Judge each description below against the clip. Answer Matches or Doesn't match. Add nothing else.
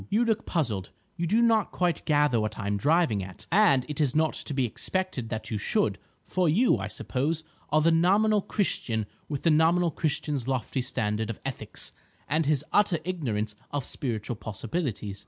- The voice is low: Doesn't match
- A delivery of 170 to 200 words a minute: Matches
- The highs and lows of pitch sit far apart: Matches